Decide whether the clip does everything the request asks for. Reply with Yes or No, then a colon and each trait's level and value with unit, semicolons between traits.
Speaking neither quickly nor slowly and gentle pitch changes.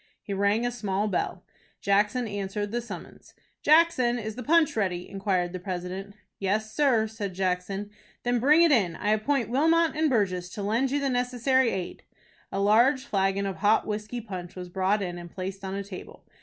No: average, 185 wpm; average, 4.2 semitones